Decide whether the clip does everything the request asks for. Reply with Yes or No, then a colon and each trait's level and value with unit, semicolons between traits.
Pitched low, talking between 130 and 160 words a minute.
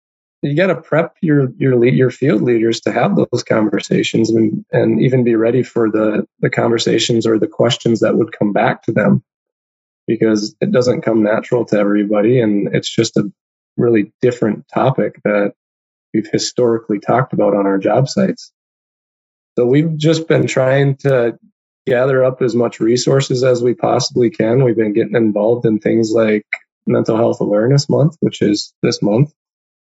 No: low, 120 Hz; average, 170 wpm